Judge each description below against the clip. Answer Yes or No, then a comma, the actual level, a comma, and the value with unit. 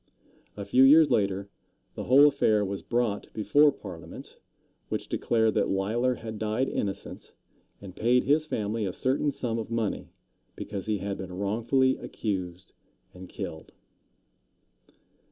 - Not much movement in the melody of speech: No, average, 4.2 semitones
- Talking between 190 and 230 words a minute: No, slow, 135 wpm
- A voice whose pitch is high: No, low, 110 Hz